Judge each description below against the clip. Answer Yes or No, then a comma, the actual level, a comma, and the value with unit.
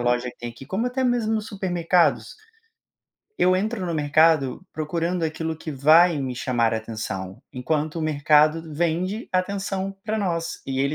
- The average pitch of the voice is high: No, medium, 160 Hz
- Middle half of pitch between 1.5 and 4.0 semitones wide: No, average, 5.0 semitones